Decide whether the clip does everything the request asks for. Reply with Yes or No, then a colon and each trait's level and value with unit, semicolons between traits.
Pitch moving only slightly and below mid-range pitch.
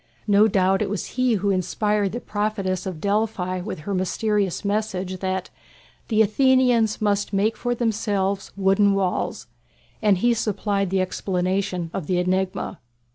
No: narrow, 2.3 semitones; high, 200 Hz